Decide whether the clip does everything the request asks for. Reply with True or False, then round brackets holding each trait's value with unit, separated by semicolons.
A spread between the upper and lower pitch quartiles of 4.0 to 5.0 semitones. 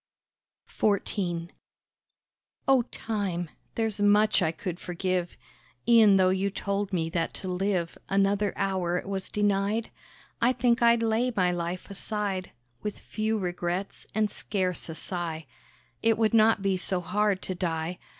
False (3.0 semitones)